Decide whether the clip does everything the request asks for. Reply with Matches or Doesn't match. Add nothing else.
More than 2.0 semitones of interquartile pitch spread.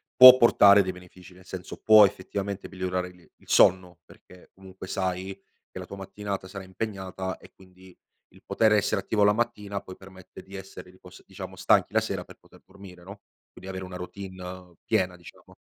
Doesn't match